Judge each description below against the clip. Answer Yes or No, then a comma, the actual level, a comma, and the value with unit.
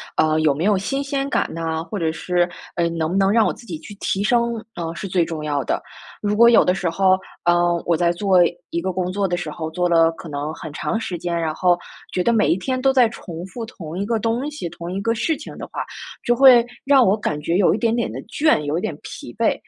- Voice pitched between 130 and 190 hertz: Yes, medium, 185 Hz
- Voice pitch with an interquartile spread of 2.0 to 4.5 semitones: No, wide, 5.4 semitones